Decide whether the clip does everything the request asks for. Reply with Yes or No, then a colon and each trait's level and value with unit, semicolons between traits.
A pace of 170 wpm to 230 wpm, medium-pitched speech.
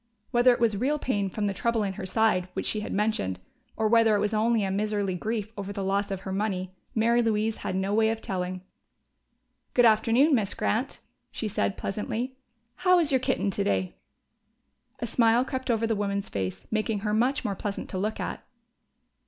No: average, 195 wpm; high, 215 Hz